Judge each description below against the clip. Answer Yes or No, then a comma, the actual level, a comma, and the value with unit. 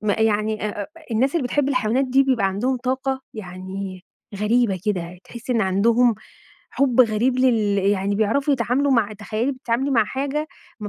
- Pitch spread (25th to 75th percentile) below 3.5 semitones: No, average, 4.1 semitones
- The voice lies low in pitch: No, high, 230 Hz